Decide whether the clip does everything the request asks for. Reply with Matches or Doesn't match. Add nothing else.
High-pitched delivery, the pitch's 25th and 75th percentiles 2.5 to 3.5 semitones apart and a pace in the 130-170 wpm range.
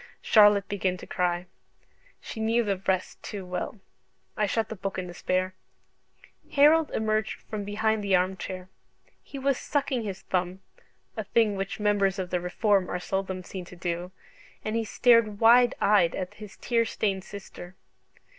Matches